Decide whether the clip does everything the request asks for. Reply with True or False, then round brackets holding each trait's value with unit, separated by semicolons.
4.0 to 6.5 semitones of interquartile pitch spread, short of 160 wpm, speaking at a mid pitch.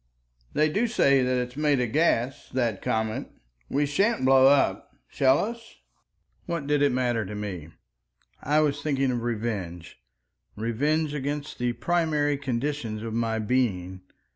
False (4.6 semitones; 145 wpm; 130 Hz)